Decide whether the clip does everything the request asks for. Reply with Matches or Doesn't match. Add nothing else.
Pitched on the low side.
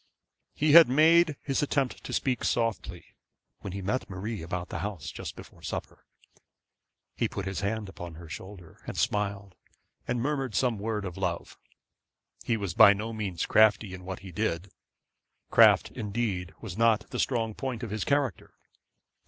Matches